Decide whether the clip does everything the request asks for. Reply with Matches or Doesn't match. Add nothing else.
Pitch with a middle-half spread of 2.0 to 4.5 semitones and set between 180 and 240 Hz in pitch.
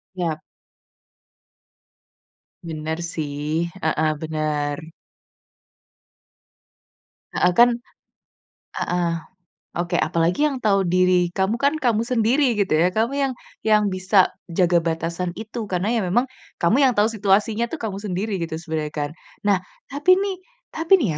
Doesn't match